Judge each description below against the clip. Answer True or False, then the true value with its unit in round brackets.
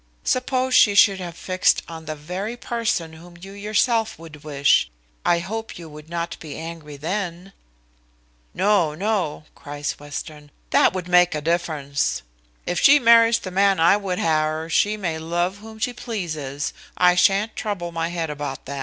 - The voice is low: False (175 Hz)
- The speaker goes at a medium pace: True (170 wpm)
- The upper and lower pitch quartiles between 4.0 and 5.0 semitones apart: True (4.6 semitones)